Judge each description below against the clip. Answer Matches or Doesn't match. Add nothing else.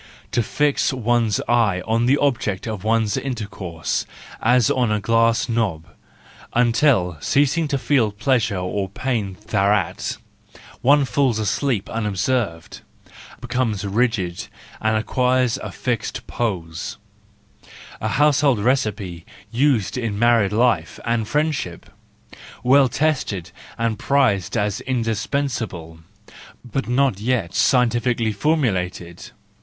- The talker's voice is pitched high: Doesn't match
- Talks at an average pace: Doesn't match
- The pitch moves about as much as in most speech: Matches